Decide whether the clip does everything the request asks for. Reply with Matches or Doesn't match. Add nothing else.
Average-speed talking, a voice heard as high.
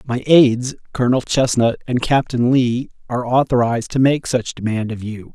Doesn't match